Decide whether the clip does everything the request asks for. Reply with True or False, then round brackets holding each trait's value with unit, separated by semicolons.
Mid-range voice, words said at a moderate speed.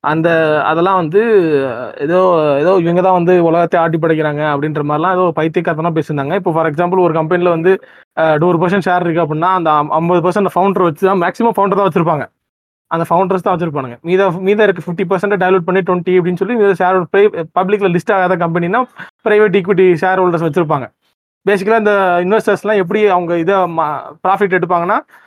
False (180 Hz; 165 wpm)